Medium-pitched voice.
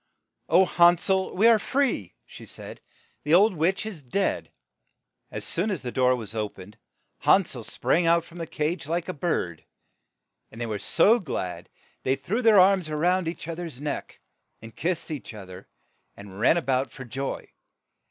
Yes: medium, 160 Hz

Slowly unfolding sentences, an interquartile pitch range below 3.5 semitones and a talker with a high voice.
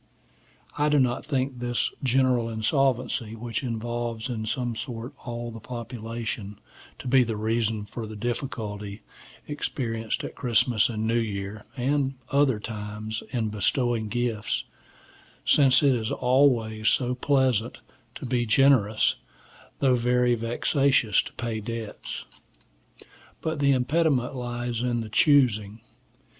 No: slow, 125 wpm; average, 2.8 semitones; low, 120 Hz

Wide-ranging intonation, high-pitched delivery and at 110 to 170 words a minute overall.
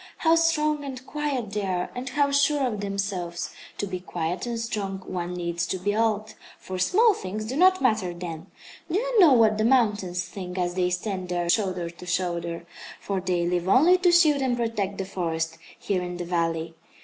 No: wide, 6.4 semitones; high, 195 Hz; average, 195 wpm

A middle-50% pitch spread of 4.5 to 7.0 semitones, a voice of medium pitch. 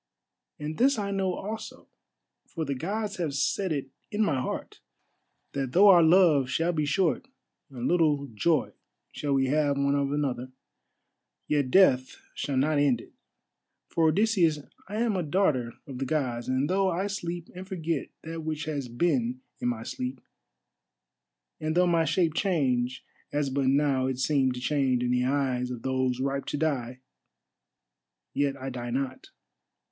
Yes: average, 4.8 semitones; medium, 145 Hz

